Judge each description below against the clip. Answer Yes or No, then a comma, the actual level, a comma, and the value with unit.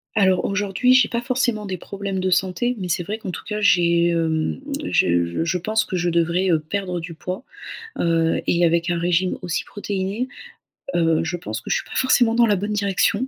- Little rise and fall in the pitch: No, average, 3.5 semitones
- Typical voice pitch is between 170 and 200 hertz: Yes, medium, 185 Hz